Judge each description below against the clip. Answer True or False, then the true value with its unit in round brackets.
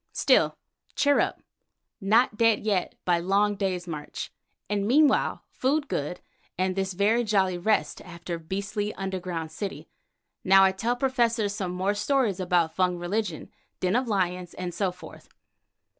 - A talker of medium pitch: False (195 Hz)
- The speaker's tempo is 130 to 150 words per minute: True (145 wpm)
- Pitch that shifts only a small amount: False (3.2 semitones)